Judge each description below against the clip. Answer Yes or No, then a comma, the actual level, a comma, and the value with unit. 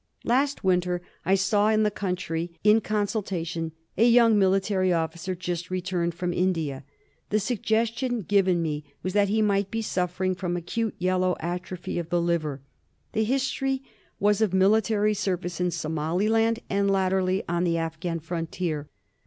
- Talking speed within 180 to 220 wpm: No, average, 150 wpm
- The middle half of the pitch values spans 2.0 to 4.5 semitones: Yes, average, 3.4 semitones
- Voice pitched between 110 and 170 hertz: No, medium, 185 Hz